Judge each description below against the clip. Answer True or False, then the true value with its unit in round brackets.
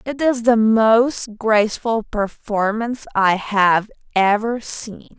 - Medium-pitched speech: False (220 Hz)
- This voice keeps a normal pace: False (115 wpm)